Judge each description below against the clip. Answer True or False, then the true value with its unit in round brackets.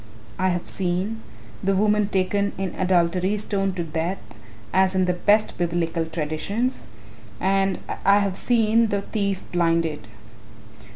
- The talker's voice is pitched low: False (190 Hz)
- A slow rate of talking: True (130 wpm)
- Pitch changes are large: False (2.6 semitones)